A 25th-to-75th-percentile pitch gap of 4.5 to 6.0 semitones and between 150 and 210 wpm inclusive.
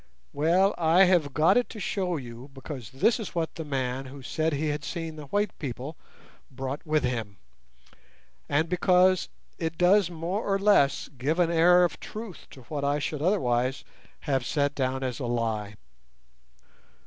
Yes: average, 5.1 semitones; average, 170 wpm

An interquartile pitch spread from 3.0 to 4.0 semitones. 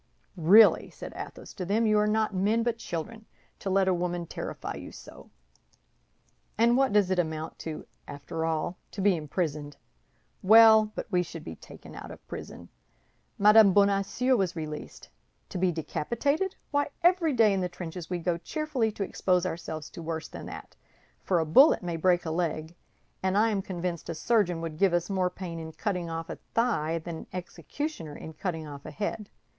No: average, 4.5 semitones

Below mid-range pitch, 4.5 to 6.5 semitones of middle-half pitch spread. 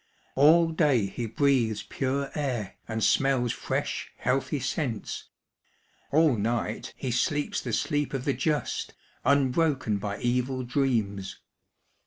No: low, 130 Hz; average, 3.6 semitones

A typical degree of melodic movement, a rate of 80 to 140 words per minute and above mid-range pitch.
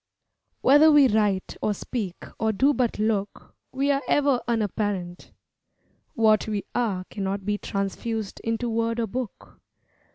Yes: average, 3.3 semitones; slow, 135 wpm; high, 220 Hz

